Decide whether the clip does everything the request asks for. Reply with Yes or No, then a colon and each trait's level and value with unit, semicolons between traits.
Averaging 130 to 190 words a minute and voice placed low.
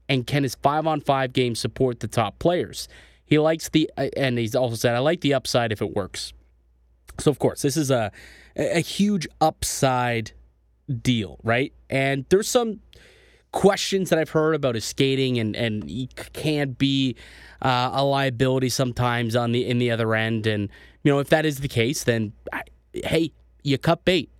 Yes: average, 180 wpm; low, 130 Hz